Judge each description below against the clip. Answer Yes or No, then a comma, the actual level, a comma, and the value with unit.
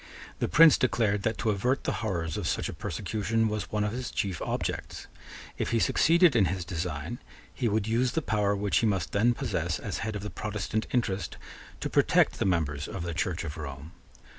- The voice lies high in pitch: No, low, 105 Hz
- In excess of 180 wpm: Yes, fast, 205 wpm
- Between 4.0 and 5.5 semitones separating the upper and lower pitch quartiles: Yes, average, 4.5 semitones